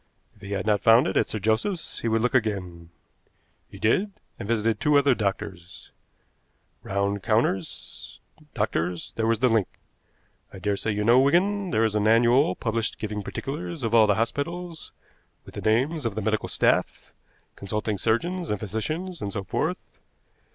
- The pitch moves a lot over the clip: No, average, 4.4 semitones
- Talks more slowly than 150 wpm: No, average, 165 wpm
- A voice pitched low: Yes, low, 110 Hz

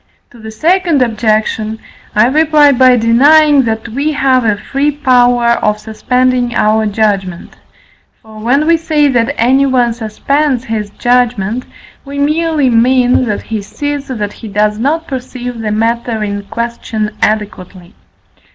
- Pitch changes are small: No, average, 4.2 semitones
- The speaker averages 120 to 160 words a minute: Yes, average, 140 wpm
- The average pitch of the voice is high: Yes, high, 240 Hz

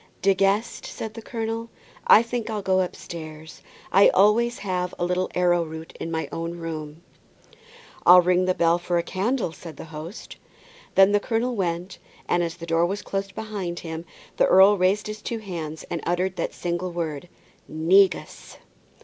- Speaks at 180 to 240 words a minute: No, average, 170 wpm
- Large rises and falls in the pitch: No, average, 3.3 semitones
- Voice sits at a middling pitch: Yes, medium, 180 Hz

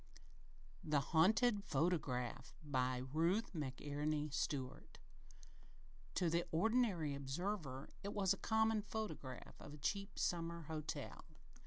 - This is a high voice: No, medium, 160 Hz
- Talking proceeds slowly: Yes, slow, 115 wpm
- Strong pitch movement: Yes, wide, 5.8 semitones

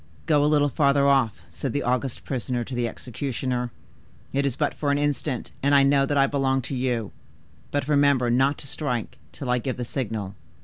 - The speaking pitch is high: No, low, 135 Hz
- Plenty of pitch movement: No, narrow, 2.4 semitones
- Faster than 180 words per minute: Yes, fast, 205 wpm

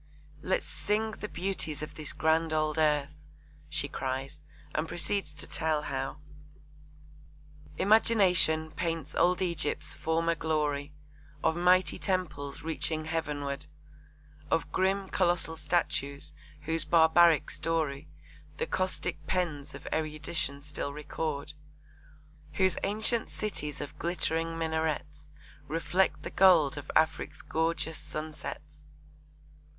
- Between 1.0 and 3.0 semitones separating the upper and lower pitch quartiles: Yes, average, 2.7 semitones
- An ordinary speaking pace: No, slow, 110 wpm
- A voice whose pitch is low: No, medium, 160 Hz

